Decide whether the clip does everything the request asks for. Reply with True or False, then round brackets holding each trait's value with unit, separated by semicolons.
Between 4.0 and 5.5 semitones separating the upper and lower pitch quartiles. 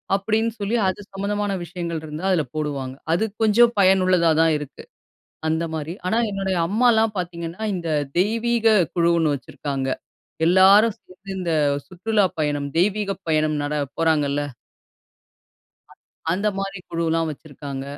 True (4.5 semitones)